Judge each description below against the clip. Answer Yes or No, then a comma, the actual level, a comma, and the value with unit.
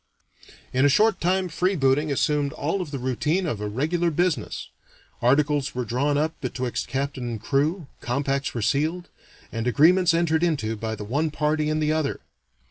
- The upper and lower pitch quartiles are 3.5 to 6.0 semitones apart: Yes, average, 3.8 semitones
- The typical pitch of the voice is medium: Yes, medium, 145 Hz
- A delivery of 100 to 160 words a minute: No, average, 170 wpm